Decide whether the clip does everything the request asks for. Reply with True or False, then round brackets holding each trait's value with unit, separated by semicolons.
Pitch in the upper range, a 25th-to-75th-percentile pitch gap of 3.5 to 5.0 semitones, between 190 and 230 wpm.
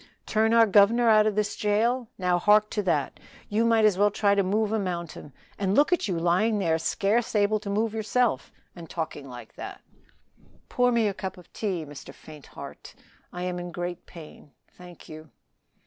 True (200 Hz; 3.8 semitones; 195 wpm)